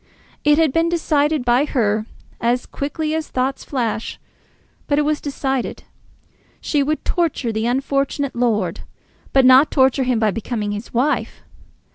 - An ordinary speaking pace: Yes, average, 145 wpm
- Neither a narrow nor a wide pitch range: Yes, average, 3.8 semitones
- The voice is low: No, very high, 265 Hz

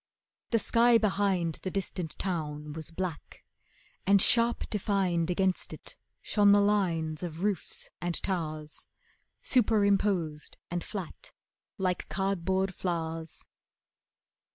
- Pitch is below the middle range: No, medium, 185 Hz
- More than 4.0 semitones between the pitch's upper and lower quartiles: No, average, 3.6 semitones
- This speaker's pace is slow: Yes, slow, 105 wpm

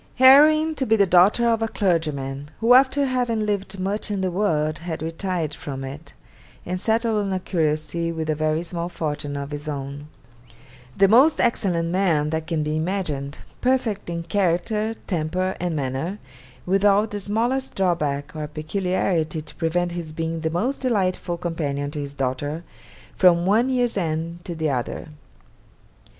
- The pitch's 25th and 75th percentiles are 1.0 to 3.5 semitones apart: No, average, 4.9 semitones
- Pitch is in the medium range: Yes, medium, 175 Hz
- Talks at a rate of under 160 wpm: No, average, 165 wpm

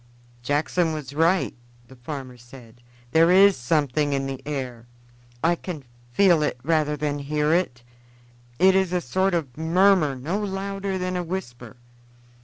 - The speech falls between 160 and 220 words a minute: No, average, 150 wpm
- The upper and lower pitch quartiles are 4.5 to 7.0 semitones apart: Yes, average, 5.3 semitones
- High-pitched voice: No, medium, 155 Hz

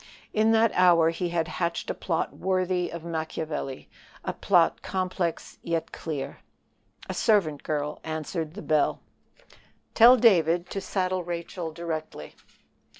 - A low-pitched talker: No, medium, 170 Hz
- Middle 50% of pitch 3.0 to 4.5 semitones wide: No, narrow, 2.6 semitones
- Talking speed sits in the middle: No, slow, 130 wpm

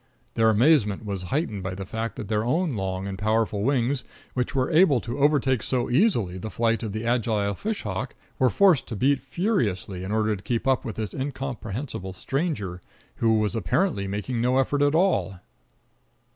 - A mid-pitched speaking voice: No, low, 115 Hz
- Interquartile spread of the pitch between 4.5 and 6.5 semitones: Yes, average, 5.1 semitones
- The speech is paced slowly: No, average, 185 wpm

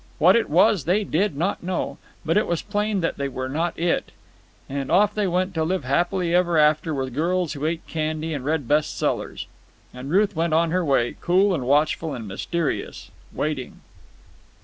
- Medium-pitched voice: Yes, medium, 165 Hz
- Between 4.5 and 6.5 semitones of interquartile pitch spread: No, average, 3.9 semitones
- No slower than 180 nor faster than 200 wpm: Yes, average, 190 wpm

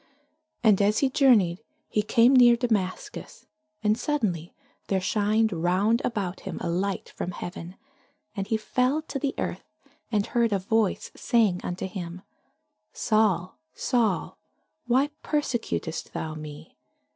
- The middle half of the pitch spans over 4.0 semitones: Yes, average, 4.5 semitones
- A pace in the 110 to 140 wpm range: Yes, slow, 135 wpm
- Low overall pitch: No, high, 210 Hz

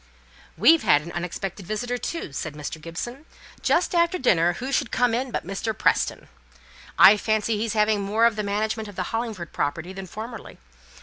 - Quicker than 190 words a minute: No, average, 180 wpm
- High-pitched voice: Yes, high, 210 Hz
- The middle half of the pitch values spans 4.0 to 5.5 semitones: Yes, average, 4.6 semitones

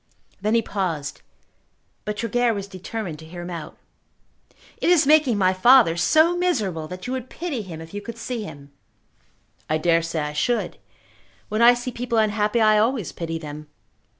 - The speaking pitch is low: No, high, 210 Hz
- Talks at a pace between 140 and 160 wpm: No, average, 175 wpm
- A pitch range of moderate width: No, wide, 6.4 semitones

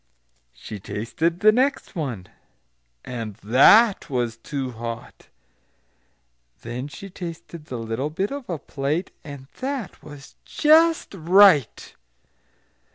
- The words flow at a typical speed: No, slow, 110 wpm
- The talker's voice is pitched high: No, medium, 150 Hz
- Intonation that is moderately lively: No, wide, 8.5 semitones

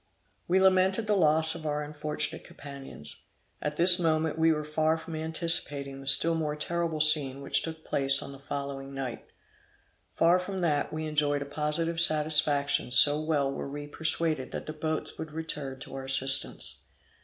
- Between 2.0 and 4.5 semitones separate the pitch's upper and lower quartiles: Yes, narrow, 2.4 semitones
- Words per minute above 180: No, average, 170 wpm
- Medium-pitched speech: Yes, medium, 150 Hz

